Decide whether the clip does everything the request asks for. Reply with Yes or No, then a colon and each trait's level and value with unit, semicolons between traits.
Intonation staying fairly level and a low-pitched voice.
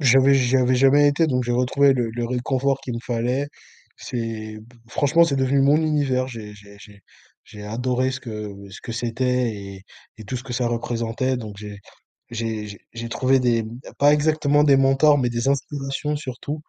No: average, 3.0 semitones; low, 125 Hz